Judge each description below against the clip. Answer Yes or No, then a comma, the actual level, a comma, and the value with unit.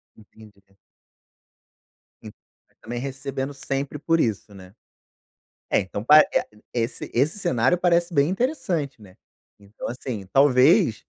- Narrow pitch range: No, average, 5.3 semitones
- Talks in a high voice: No, low, 135 Hz